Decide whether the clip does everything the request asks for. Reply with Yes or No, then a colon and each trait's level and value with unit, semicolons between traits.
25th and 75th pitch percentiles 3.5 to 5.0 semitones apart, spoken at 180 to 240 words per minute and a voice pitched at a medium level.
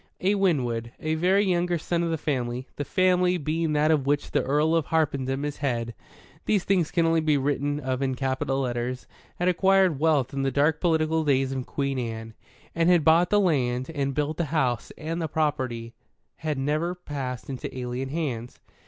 Yes: average, 3.9 semitones; average, 190 wpm; medium, 150 Hz